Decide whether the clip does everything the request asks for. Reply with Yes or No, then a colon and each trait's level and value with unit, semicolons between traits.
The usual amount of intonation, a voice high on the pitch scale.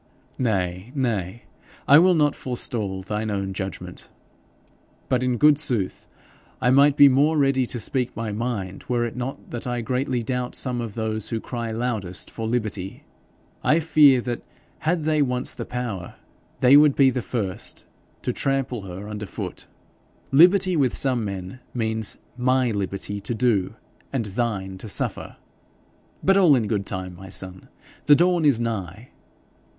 No: average, 4.7 semitones; low, 120 Hz